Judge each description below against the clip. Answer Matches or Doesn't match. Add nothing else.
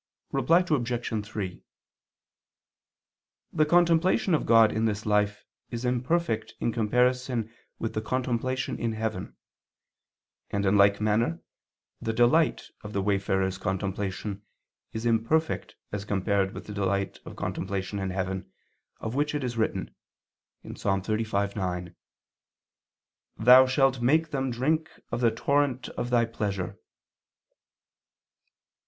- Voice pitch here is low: Matches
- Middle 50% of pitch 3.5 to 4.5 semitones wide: Matches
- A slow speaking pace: Matches